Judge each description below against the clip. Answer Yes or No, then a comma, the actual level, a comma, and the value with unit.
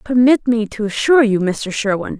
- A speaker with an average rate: Yes, average, 190 wpm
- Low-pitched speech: No, high, 230 Hz